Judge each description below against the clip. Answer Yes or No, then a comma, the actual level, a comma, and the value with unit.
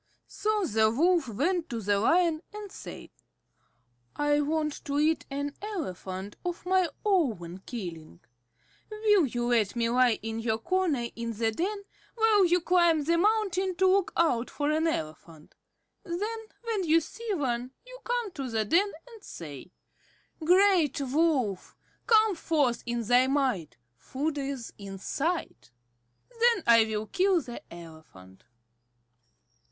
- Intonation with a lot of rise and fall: Yes, wide, 8.4 semitones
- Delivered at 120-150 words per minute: Yes, average, 140 wpm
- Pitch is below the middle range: No, very high, 295 Hz